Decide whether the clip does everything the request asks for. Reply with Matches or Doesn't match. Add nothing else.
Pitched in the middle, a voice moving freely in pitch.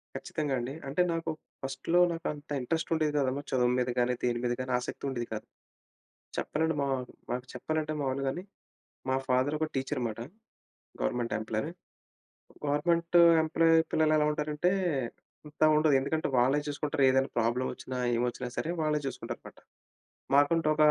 Doesn't match